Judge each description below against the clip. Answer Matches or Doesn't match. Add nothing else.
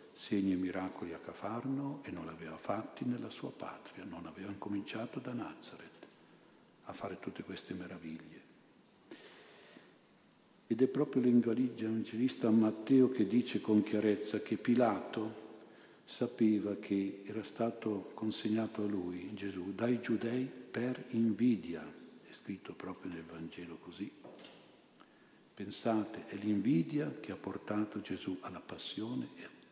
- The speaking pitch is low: Matches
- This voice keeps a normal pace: Matches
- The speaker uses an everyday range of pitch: Matches